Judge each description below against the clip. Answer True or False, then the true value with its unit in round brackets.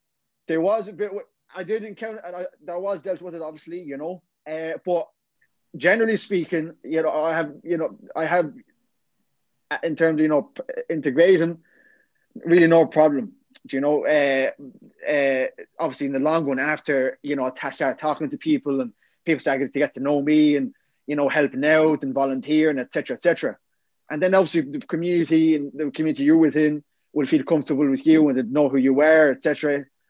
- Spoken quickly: False (185 wpm)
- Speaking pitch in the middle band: True (160 Hz)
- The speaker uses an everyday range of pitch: True (3.6 semitones)